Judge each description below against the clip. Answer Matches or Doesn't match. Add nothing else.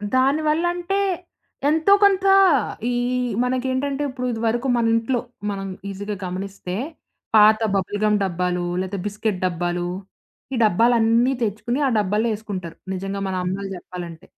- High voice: Matches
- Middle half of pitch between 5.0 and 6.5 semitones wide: Matches